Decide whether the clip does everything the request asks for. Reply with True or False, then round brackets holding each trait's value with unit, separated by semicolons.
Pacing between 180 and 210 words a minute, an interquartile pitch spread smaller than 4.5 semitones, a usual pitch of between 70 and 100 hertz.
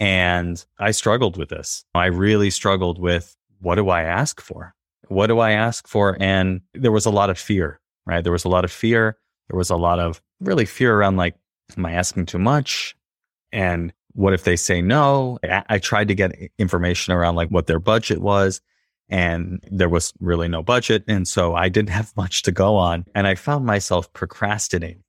True (200 wpm; 3.1 semitones; 95 Hz)